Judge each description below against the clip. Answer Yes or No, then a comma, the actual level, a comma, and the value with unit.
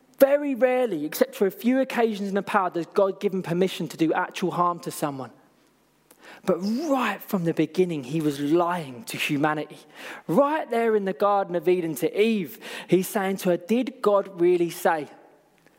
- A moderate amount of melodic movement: Yes, average, 4.9 semitones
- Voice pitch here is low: No, high, 190 Hz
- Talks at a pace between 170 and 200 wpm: Yes, average, 180 wpm